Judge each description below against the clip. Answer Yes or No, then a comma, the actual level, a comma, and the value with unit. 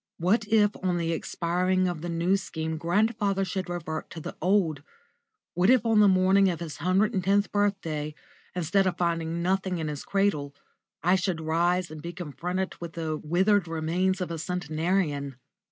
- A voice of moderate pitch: Yes, medium, 180 Hz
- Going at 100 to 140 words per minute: No, average, 175 wpm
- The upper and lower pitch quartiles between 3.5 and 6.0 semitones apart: No, average, 2.9 semitones